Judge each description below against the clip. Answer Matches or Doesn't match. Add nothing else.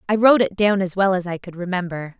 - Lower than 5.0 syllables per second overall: Doesn't match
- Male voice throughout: Doesn't match